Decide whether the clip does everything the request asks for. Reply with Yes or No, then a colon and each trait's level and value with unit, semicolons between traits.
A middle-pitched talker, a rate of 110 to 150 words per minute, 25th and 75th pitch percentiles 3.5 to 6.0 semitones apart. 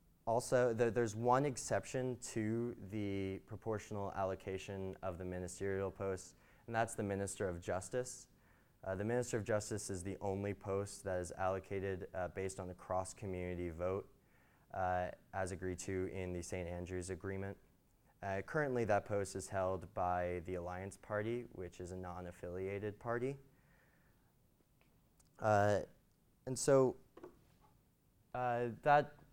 No: low, 100 Hz; average, 140 wpm; average, 3.9 semitones